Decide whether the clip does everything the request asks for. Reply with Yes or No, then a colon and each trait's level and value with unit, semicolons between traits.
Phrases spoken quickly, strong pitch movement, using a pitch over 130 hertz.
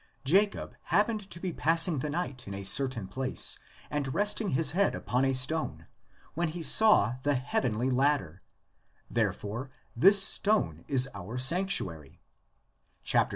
No: average, 145 wpm; wide, 6.2 semitones; medium, 140 Hz